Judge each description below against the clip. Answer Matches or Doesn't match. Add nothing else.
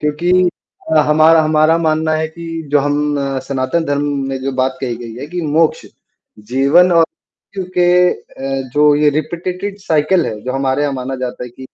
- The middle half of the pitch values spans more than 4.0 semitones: Doesn't match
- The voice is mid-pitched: Matches